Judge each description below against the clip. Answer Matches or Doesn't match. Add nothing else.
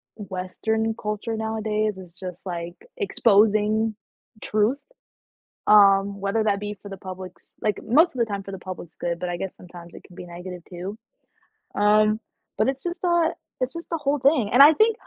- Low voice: Doesn't match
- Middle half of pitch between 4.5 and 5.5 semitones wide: Doesn't match